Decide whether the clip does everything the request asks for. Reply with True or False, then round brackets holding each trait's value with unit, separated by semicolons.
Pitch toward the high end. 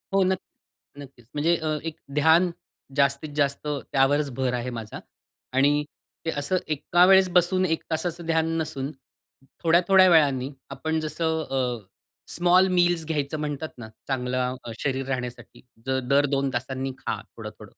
False (150 Hz)